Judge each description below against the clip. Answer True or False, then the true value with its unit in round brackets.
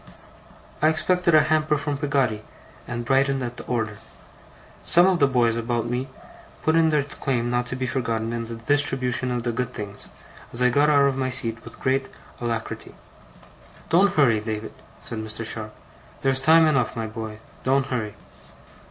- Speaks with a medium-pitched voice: False (125 Hz)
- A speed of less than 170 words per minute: False (175 wpm)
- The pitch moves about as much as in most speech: True (3.7 semitones)